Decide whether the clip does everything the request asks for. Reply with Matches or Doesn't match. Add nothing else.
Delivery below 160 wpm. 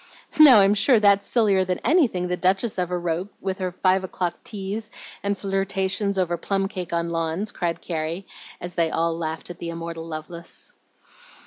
Doesn't match